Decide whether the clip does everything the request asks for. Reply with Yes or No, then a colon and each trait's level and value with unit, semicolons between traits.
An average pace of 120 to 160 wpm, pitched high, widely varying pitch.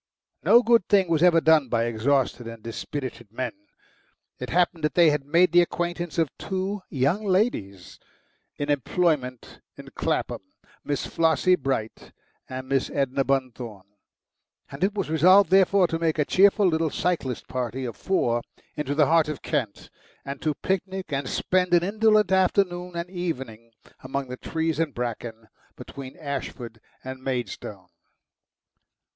No: average, 150 wpm; medium, 150 Hz; wide, 5.7 semitones